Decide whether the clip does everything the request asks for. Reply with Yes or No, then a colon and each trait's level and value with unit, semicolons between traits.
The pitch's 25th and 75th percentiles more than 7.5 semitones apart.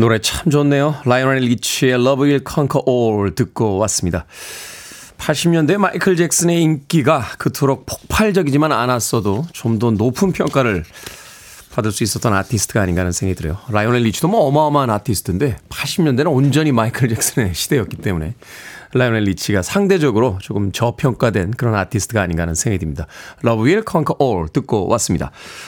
No: wide, 5.4 semitones